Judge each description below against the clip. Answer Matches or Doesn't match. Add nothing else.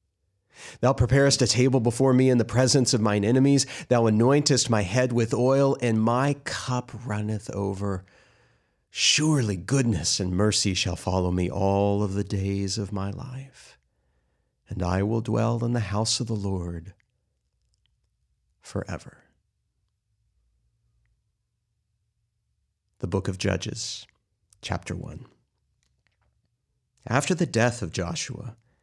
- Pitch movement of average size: Matches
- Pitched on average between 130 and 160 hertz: Doesn't match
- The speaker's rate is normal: Doesn't match